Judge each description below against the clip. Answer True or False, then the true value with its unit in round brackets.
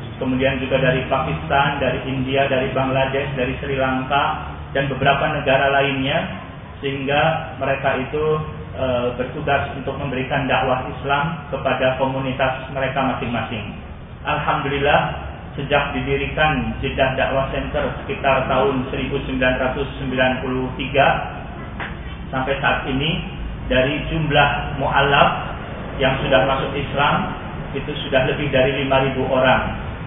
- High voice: False (135 Hz)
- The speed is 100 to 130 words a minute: True (105 wpm)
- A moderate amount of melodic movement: False (1.2 semitones)